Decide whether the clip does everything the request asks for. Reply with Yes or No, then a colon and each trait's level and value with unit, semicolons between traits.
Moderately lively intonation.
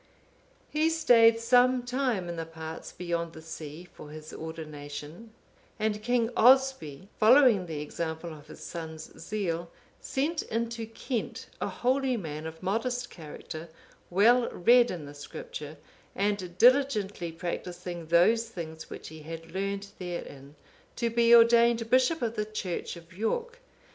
No: wide, 6.4 semitones